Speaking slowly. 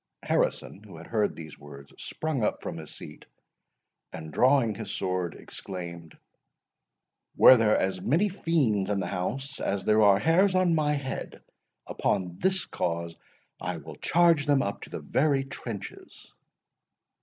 No: average, 145 wpm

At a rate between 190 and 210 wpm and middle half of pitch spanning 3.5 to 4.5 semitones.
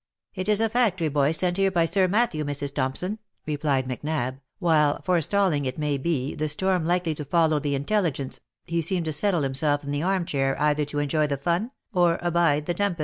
Yes: fast, 205 wpm; average, 3.8 semitones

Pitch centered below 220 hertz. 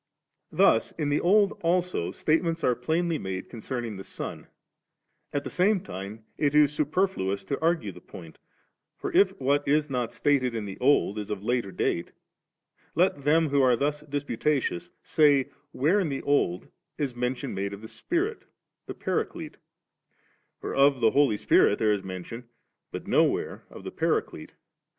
Yes: medium, 140 Hz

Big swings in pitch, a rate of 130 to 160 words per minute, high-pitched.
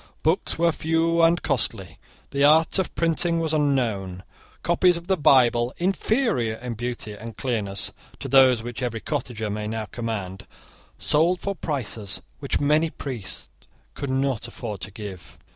No: wide, 6.5 semitones; average, 150 wpm; low, 130 Hz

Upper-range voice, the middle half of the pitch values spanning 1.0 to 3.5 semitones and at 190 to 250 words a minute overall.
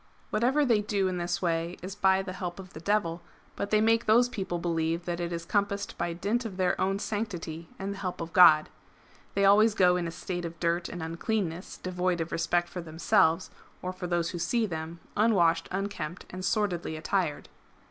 No: medium, 180 Hz; average, 3.0 semitones; average, 200 wpm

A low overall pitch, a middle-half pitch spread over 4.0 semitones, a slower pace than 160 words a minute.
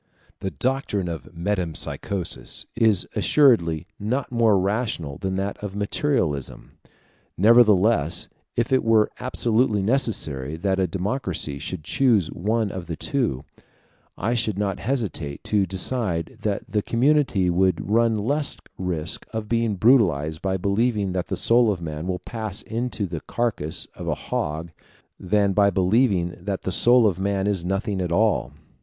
Yes: low, 100 Hz; average, 4.4 semitones; average, 150 wpm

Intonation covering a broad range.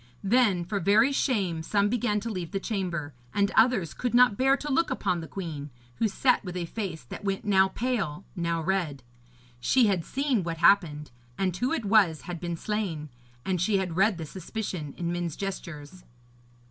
No: average, 4.4 semitones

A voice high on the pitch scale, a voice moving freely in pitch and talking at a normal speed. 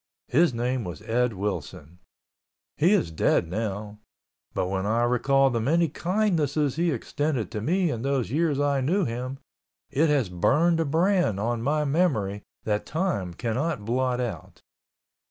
No: low, 125 Hz; wide, 6.6 semitones; average, 150 wpm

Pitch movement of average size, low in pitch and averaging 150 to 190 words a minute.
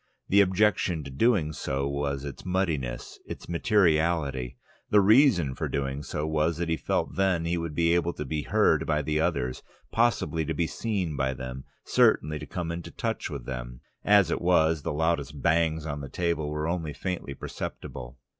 Yes: average, 3.5 semitones; very low, 80 Hz; average, 185 wpm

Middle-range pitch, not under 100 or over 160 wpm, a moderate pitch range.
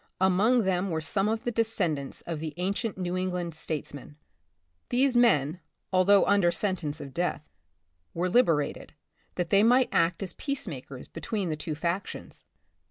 Yes: medium, 180 Hz; average, 155 wpm; average, 4.3 semitones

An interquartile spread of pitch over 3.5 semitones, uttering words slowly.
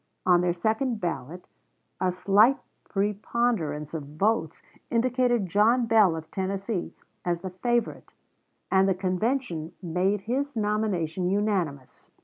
Yes: average, 4.3 semitones; slow, 120 wpm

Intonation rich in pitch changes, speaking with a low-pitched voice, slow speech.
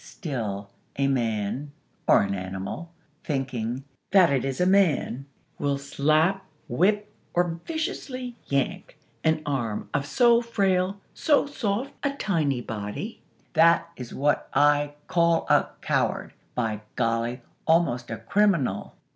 No: wide, 7.8 semitones; medium, 145 Hz; slow, 125 wpm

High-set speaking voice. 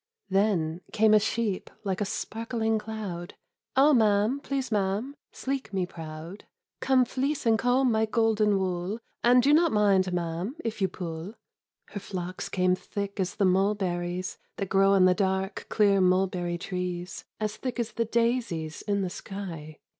Yes: high, 200 Hz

